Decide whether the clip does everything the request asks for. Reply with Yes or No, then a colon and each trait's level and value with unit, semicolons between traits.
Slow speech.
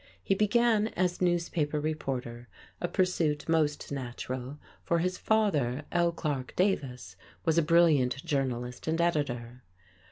Yes: slow, 125 wpm